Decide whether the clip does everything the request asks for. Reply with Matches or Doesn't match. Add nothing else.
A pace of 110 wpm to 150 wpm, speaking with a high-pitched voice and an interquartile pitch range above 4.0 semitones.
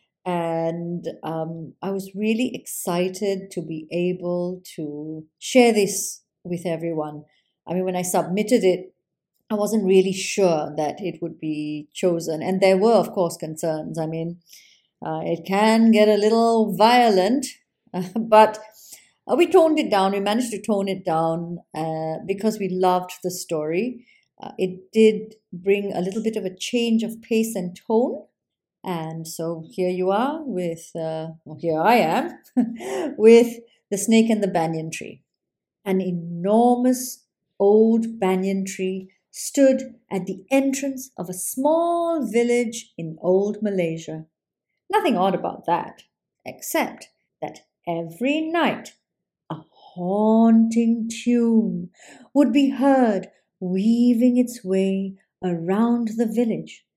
Matches